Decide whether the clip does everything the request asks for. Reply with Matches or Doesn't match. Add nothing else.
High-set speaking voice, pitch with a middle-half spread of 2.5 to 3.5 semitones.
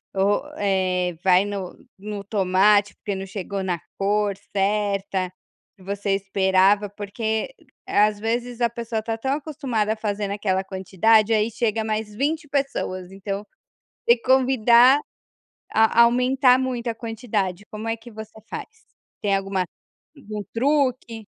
Matches